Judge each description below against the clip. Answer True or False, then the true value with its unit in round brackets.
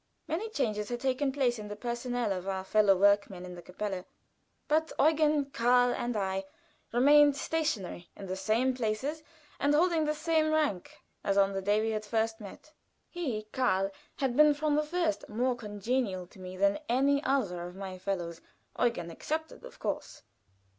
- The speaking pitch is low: False (235 Hz)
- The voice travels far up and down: True (6.7 semitones)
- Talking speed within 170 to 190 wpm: True (175 wpm)